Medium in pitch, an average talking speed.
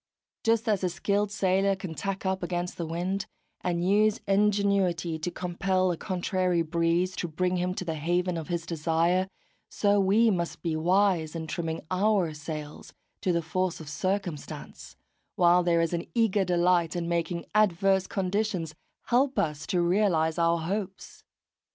Yes: medium, 180 Hz; average, 160 wpm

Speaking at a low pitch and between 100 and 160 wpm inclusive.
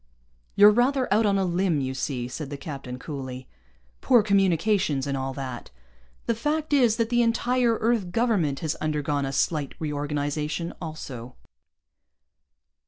No: medium, 160 Hz; average, 145 wpm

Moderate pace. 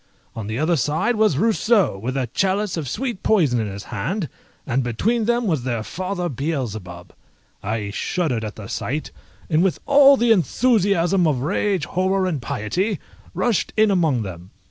Yes: average, 165 wpm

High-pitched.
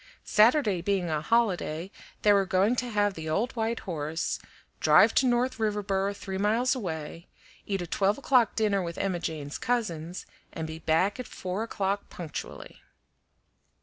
Yes: high, 195 Hz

